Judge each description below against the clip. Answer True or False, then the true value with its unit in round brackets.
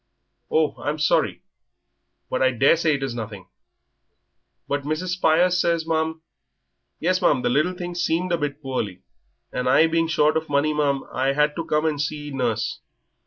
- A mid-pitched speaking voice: True (150 Hz)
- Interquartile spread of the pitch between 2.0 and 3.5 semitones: True (3.1 semitones)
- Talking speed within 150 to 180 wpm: True (170 wpm)